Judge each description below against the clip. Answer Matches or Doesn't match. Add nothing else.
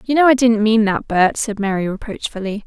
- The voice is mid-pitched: Doesn't match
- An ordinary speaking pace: Doesn't match